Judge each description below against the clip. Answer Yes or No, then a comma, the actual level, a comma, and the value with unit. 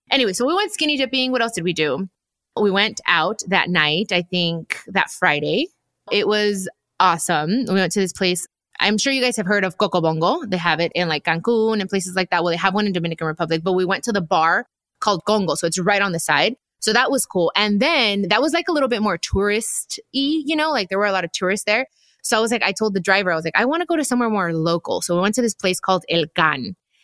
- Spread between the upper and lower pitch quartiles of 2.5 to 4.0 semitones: No, average, 4.6 semitones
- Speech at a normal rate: No, fast, 265 wpm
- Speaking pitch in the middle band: No, high, 200 Hz